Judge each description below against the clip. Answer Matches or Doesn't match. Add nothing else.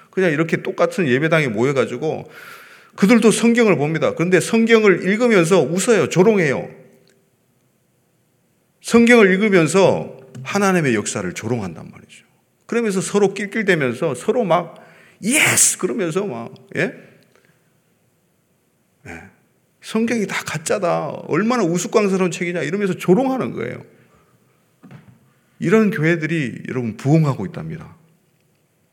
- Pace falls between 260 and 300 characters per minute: Matches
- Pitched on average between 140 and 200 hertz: Matches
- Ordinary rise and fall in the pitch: Matches